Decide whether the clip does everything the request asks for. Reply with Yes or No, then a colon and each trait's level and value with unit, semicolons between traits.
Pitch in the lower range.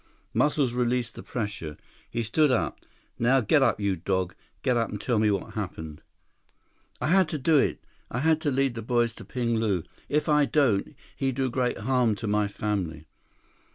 Yes: low, 120 Hz